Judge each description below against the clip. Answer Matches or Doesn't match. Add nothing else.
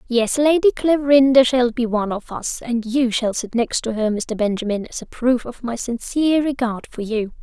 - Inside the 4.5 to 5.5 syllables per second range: Matches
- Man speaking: Doesn't match